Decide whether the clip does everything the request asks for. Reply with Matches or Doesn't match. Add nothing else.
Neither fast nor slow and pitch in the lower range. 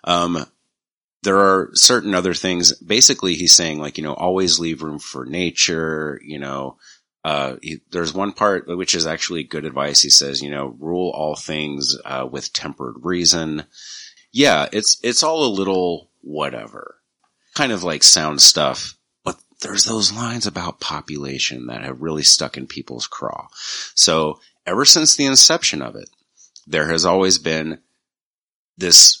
Matches